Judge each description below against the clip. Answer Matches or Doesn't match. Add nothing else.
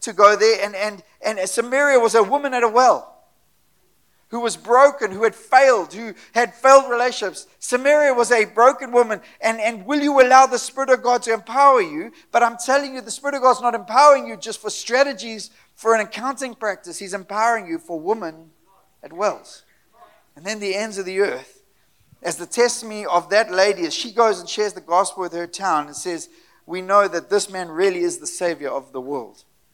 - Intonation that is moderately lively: Matches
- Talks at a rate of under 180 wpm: Doesn't match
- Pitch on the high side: Matches